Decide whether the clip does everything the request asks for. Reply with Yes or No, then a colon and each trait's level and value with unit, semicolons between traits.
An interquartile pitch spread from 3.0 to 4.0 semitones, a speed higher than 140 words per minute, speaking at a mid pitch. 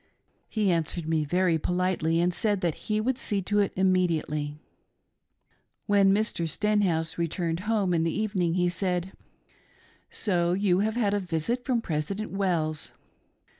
Yes: average, 3.7 semitones; average, 155 wpm; medium, 180 Hz